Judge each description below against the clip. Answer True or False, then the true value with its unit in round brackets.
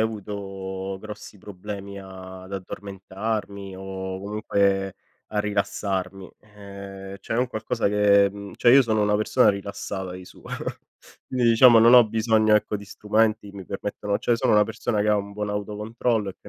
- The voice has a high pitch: False (105 Hz)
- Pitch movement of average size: False (1.8 semitones)